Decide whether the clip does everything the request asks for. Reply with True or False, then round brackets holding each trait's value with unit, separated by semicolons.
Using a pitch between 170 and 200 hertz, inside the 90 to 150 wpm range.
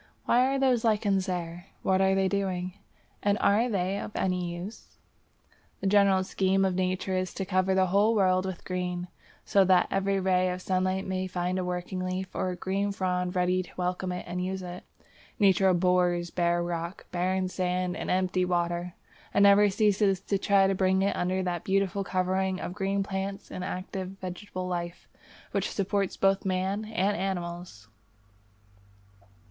False (185 Hz; 170 wpm)